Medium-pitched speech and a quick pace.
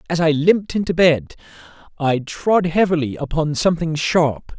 No: medium, 160 Hz; average, 145 wpm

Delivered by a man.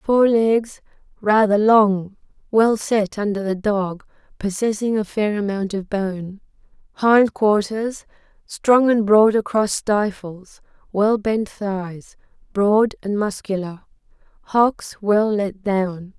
No: female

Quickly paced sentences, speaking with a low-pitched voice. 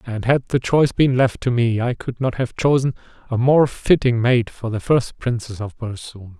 Yes: fast, 215 wpm; low, 120 Hz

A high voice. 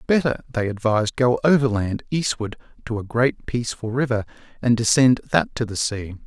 No: low, 120 Hz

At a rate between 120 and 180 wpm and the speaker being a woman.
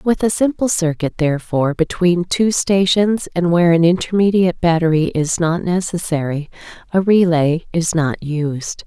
Yes: average, 140 wpm; female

